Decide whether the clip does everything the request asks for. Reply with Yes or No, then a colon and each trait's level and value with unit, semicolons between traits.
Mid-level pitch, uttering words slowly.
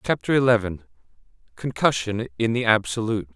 No: low, 115 Hz; slow, 90 wpm